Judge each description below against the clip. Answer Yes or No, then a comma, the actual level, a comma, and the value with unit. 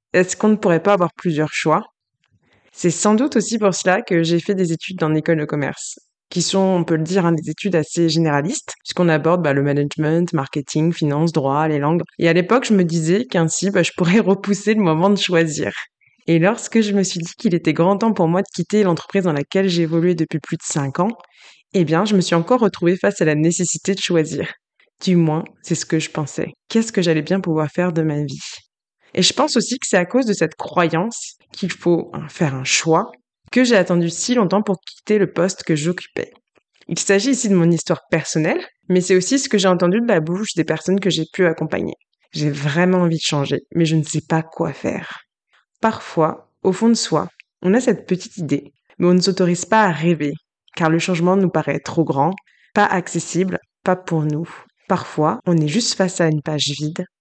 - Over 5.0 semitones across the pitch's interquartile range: No, average, 3.3 semitones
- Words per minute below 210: No, fast, 220 wpm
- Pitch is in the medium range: Yes, medium, 175 Hz